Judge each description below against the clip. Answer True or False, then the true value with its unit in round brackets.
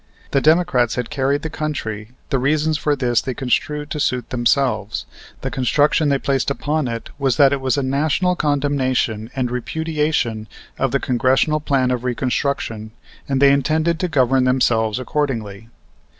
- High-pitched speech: False (135 Hz)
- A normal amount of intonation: True (3.1 semitones)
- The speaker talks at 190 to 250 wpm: False (160 wpm)